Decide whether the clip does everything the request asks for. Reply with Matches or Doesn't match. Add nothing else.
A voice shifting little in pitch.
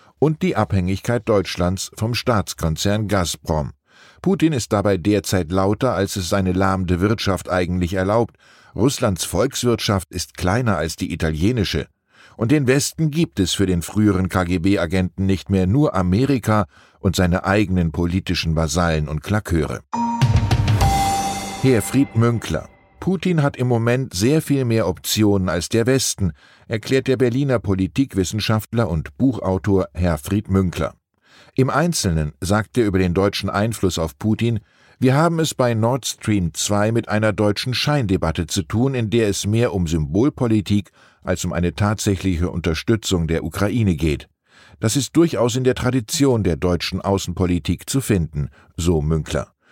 Doesn't match